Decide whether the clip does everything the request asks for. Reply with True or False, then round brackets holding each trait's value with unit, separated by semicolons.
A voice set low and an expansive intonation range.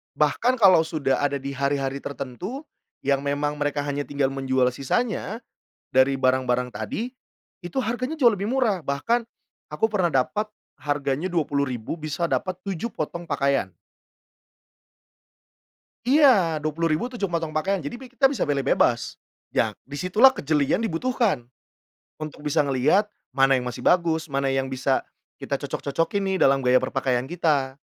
False (150 Hz; 6.2 semitones)